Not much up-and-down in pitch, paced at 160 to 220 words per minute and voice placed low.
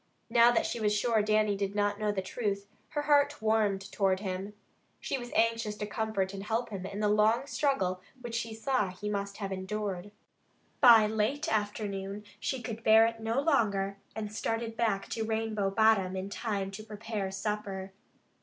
No: narrow, 2.3 semitones; average, 180 wpm; high, 210 Hz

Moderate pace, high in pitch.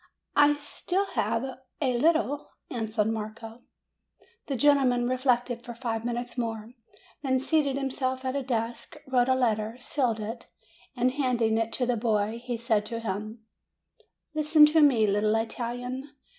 Yes: average, 145 wpm; high, 245 Hz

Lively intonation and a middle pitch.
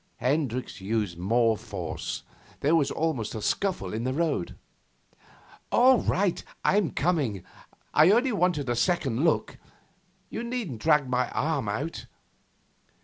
Yes: wide, 7.4 semitones; medium, 145 Hz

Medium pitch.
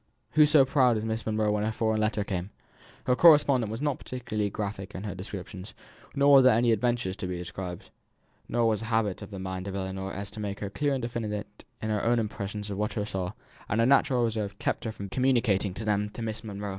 No: low, 105 Hz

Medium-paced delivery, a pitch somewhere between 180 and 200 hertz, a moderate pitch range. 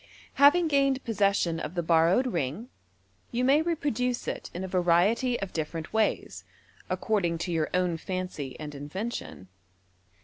No: average, 145 wpm; high, 190 Hz; wide, 6.9 semitones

